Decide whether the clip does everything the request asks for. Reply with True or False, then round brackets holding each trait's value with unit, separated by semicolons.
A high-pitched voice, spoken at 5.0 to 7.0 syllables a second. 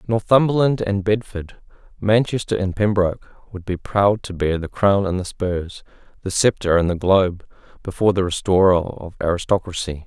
False (95 Hz; 5.1 syllables/s)